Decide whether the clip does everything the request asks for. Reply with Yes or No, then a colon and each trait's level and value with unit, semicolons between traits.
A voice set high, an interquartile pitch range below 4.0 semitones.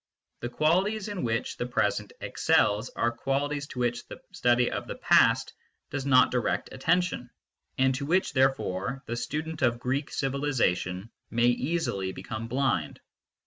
No: low, 130 Hz; average, 3.4 semitones